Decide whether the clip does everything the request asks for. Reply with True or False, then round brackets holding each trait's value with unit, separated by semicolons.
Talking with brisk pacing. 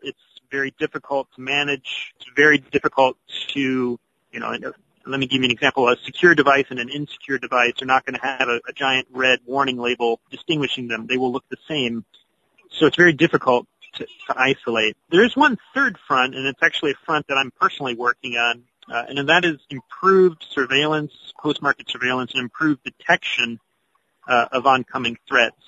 False (185 wpm)